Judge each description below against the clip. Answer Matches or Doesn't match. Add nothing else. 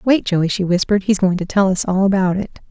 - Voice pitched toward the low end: Doesn't match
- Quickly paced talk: Matches